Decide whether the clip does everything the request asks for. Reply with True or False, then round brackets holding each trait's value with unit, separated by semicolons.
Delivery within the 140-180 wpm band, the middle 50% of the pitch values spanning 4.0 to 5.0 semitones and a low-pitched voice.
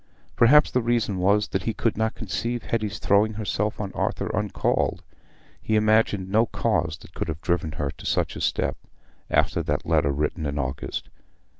True (175 wpm; 4.6 semitones; 105 Hz)